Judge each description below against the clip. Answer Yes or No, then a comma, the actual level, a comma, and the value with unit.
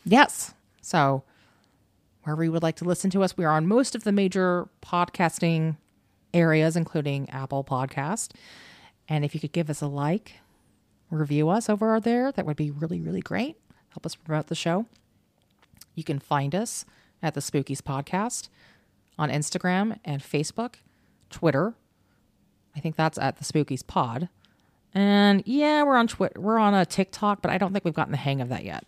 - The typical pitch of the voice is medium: Yes, medium, 165 Hz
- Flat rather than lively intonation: No, average, 5.2 semitones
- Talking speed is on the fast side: No, average, 175 wpm